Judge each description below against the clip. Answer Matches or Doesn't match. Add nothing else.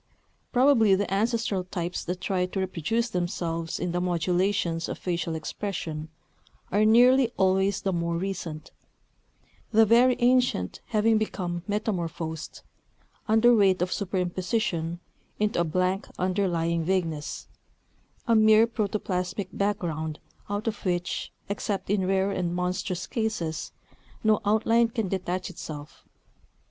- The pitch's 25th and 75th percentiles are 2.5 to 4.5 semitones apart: Matches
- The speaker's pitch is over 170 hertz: Matches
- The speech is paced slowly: Matches